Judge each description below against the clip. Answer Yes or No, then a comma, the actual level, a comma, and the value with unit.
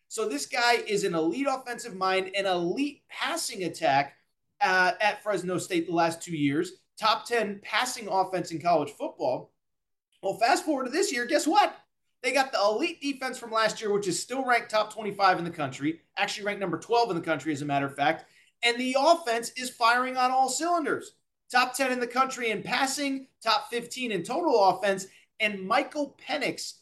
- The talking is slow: No, average, 195 wpm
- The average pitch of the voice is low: No, high, 220 Hz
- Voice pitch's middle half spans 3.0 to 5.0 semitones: No, wide, 5.5 semitones